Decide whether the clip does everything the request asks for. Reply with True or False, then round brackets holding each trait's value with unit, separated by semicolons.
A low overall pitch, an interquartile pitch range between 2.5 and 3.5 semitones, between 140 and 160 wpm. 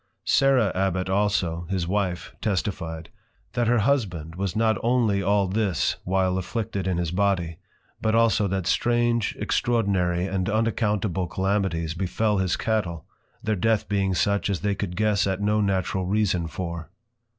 True (100 Hz; 2.9 semitones; 150 wpm)